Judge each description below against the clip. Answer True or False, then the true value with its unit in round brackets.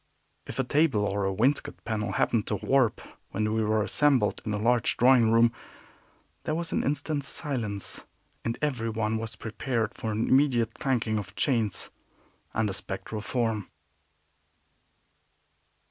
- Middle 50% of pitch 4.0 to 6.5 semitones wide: False (3.5 semitones)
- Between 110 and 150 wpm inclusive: True (145 wpm)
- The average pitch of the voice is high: False (115 Hz)